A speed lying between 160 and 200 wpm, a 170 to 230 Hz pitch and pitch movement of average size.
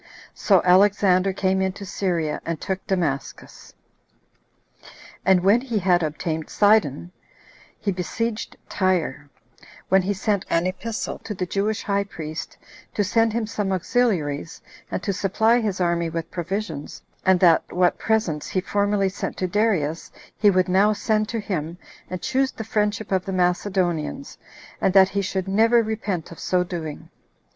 No: average, 150 wpm; high, 190 Hz; average, 3.1 semitones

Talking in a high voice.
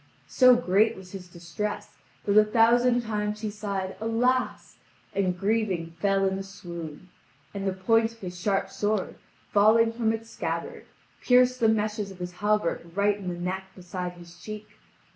Yes: high, 205 Hz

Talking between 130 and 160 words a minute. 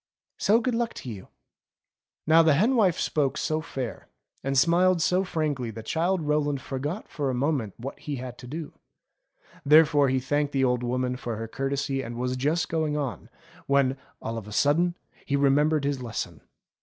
No: average, 185 wpm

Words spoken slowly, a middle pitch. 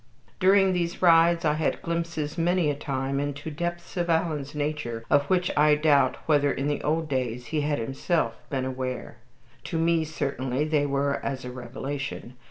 No: average, 175 wpm; medium, 150 Hz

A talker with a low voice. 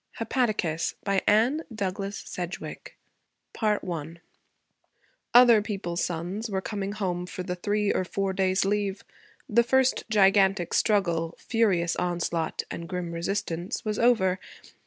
No: high, 195 Hz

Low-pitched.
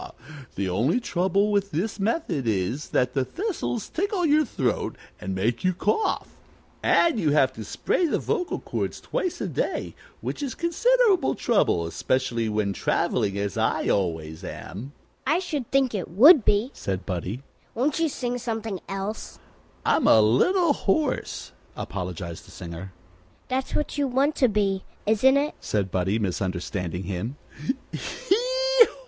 No: high, 190 Hz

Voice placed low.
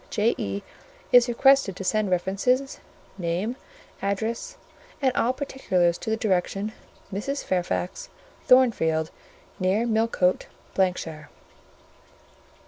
No: high, 210 Hz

